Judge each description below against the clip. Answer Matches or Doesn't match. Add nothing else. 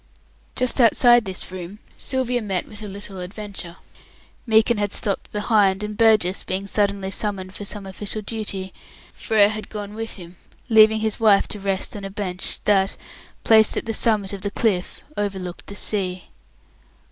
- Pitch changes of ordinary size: Doesn't match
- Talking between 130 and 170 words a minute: Matches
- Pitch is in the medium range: Doesn't match